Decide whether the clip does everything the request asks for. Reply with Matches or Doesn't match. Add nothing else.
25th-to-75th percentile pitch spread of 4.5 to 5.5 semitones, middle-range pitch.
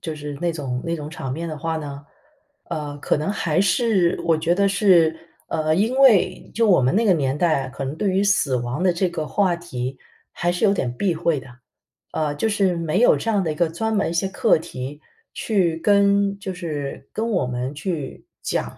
Matches